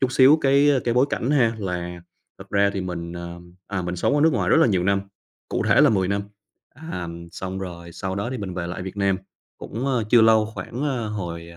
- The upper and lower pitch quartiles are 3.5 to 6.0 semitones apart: Yes, wide, 5.6 semitones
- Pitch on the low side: Yes, low, 100 Hz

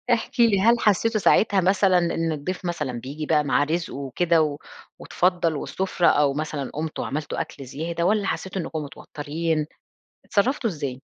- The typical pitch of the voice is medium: Yes, medium, 165 Hz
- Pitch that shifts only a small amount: No, average, 4.3 semitones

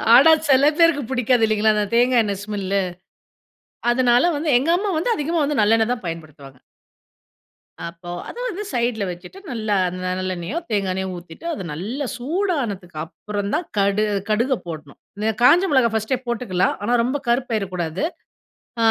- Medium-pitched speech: No, high, 220 Hz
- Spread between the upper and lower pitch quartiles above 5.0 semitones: Yes, wide, 5.6 semitones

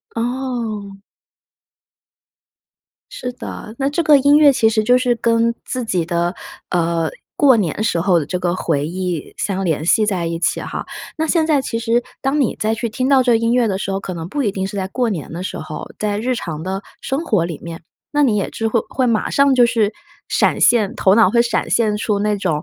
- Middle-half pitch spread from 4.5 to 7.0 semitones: Yes, average, 5.1 semitones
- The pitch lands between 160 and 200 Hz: No, high, 215 Hz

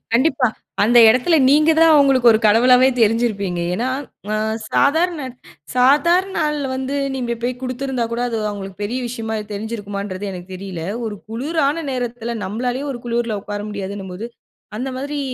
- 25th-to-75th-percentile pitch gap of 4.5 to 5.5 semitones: Yes, average, 4.8 semitones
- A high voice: Yes, high, 240 Hz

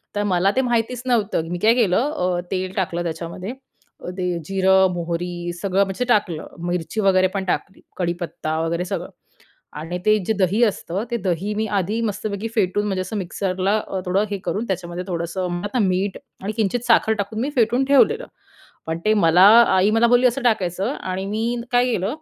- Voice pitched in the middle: No, high, 195 Hz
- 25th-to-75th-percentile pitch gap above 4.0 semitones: No, average, 3.6 semitones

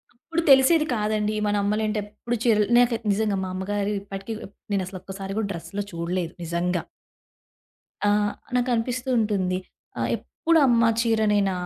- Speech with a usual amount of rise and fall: Yes, average, 3.2 semitones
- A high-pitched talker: Yes, high, 210 Hz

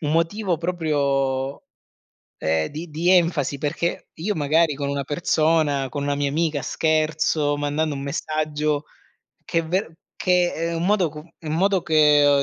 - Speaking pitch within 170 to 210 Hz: No, medium, 155 Hz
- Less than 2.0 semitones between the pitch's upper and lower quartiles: No, narrow, 2.6 semitones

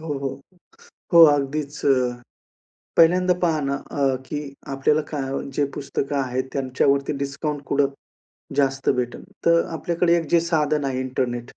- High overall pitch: No, medium, 140 Hz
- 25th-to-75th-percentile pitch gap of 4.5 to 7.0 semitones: No, narrow, 2.4 semitones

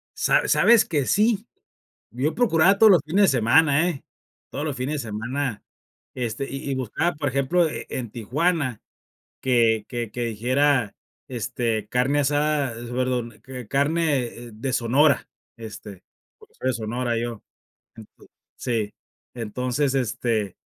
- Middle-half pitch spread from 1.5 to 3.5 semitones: No, average, 3.9 semitones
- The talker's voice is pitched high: No, low, 130 Hz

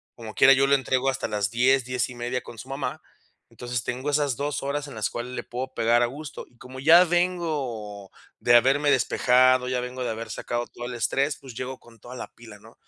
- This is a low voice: Yes, low, 125 Hz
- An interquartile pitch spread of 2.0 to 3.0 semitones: Yes, narrow, 2.4 semitones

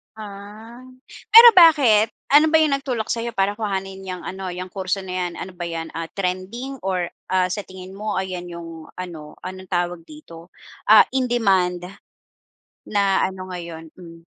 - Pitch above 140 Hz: Yes, high, 190 Hz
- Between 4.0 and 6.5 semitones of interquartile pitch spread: No, average, 3.6 semitones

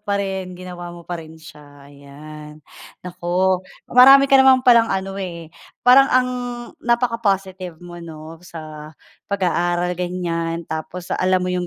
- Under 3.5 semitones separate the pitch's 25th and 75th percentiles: Yes, average, 2.9 semitones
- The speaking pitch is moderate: Yes, medium, 180 Hz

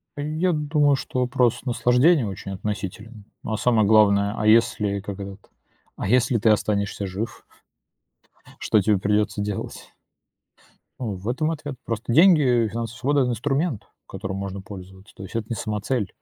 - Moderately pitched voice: No, low, 110 Hz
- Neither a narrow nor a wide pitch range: Yes, average, 3.9 semitones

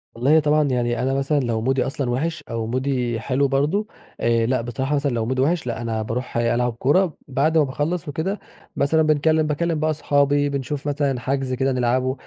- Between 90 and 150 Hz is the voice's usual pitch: Yes, low, 135 Hz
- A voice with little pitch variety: No, average, 3.3 semitones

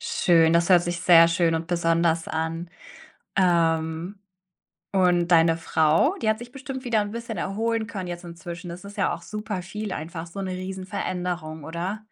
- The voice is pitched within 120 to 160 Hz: No, medium, 175 Hz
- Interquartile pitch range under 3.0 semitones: No, average, 3.4 semitones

